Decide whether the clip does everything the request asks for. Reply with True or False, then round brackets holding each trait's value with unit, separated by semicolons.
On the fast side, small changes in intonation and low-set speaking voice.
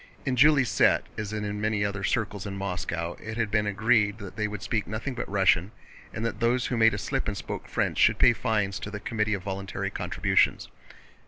True (215 wpm; 2.2 semitones; 105 Hz)